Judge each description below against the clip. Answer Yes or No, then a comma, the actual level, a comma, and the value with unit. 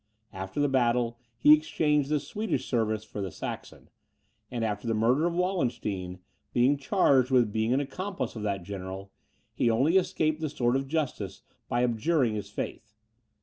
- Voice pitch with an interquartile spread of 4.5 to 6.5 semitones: Yes, wide, 5.6 semitones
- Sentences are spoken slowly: No, average, 165 wpm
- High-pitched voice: No, low, 120 Hz